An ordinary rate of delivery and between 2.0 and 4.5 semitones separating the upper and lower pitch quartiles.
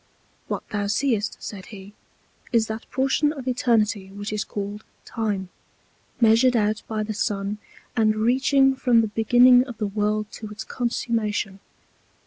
Yes: average, 145 wpm; average, 2.8 semitones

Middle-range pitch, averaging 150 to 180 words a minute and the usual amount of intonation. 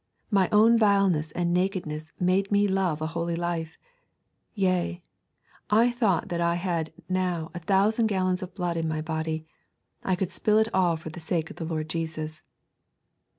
Yes: medium, 175 Hz; average, 170 wpm; average, 3.2 semitones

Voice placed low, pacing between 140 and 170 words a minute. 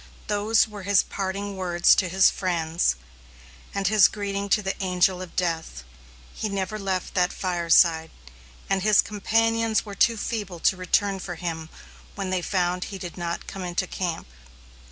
No: high, 190 Hz; average, 160 wpm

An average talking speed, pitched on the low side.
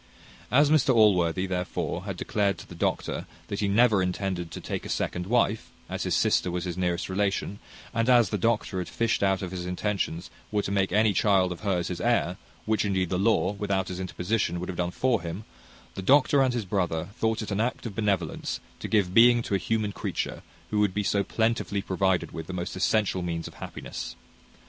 No: fast, 210 wpm; low, 100 Hz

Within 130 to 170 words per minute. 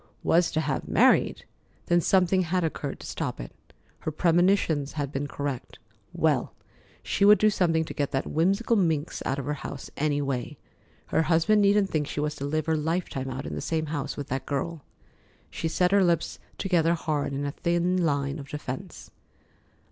No: average, 185 wpm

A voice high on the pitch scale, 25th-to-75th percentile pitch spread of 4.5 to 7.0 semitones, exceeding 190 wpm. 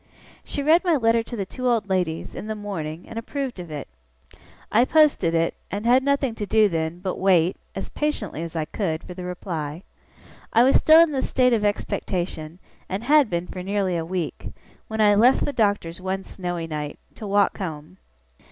Yes: high, 195 Hz; wide, 5.4 semitones; average, 200 wpm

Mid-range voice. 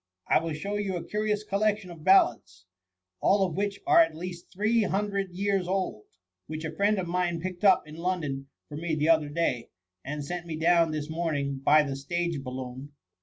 Yes: medium, 170 Hz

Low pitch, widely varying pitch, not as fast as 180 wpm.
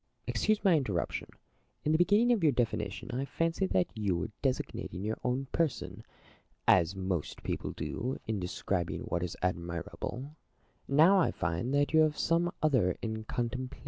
Yes: low, 125 Hz; wide, 8.6 semitones; average, 165 wpm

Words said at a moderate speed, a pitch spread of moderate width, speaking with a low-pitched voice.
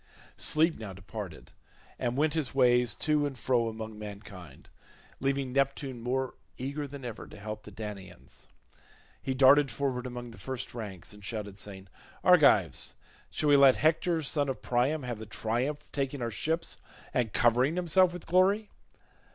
Yes: average, 160 wpm; average, 4.8 semitones; low, 125 Hz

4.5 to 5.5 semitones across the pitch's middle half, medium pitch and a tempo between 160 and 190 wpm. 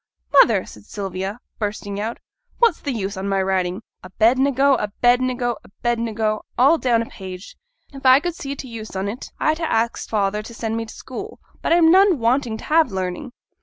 No: average, 5.0 semitones; high, 230 Hz; average, 185 wpm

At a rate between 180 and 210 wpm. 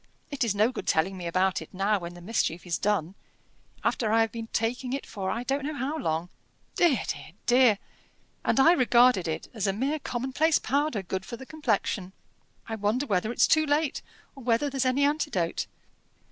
Yes: average, 195 wpm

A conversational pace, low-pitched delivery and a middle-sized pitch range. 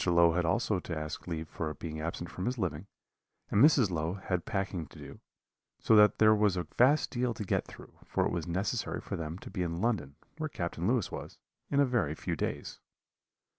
No: fast, 210 wpm; very low, 90 Hz; average, 4.8 semitones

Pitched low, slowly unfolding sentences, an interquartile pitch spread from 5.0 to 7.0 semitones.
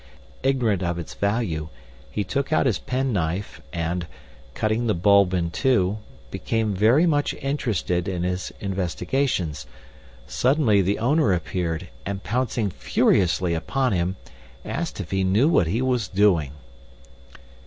Yes: low, 100 Hz; slow, 130 wpm; wide, 5.6 semitones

